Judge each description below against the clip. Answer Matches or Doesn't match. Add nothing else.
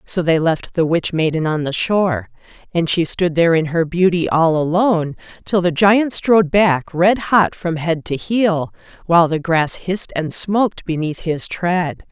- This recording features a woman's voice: Matches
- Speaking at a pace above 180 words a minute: Matches